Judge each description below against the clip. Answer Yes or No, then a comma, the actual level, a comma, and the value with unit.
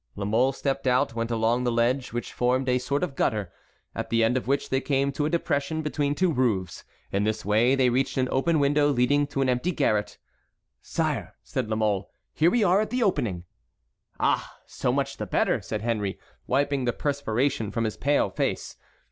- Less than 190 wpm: No, average, 200 wpm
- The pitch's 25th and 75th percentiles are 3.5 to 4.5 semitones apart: Yes, average, 3.8 semitones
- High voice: No, low, 130 Hz